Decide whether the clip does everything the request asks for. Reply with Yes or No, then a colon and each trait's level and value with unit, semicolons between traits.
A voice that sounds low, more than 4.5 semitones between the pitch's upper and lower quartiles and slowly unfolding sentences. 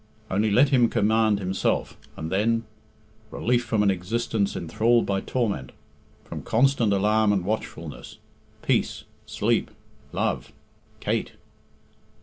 No: low, 110 Hz; average, 2.9 semitones; slow, 115 wpm